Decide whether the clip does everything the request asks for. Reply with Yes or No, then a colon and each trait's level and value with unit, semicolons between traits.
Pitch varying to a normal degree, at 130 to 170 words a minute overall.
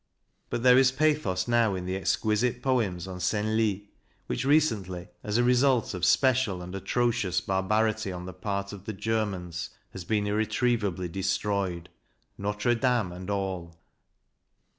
Yes: average, 4.1 semitones; average, 140 wpm